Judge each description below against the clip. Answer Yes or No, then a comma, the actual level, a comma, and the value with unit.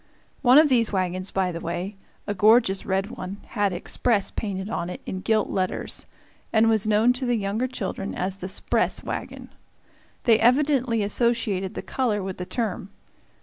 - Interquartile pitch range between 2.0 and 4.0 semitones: Yes, average, 3.6 semitones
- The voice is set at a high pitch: Yes, high, 205 Hz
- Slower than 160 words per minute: No, average, 170 wpm